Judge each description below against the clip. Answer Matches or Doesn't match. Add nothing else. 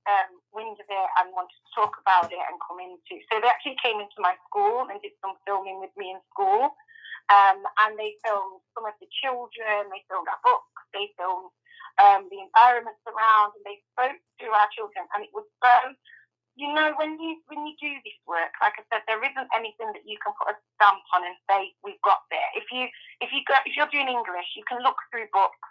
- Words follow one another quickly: Matches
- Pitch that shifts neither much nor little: Doesn't match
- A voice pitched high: Matches